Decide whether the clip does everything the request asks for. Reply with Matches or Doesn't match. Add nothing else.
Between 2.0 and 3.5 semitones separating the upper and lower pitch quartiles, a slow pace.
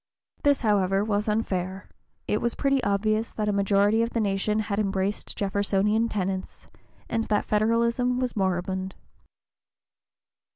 Matches